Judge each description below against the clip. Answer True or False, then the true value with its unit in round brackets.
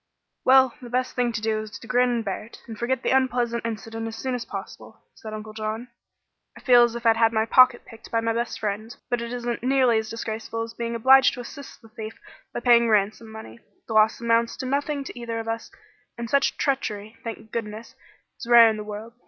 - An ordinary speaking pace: False (225 wpm)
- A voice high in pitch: True (230 Hz)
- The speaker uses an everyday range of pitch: False (1.8 semitones)